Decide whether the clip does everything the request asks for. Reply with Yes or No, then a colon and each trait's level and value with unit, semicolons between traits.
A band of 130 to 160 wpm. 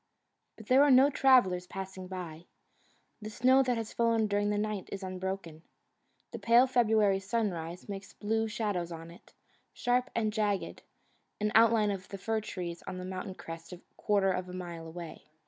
No: average, 170 wpm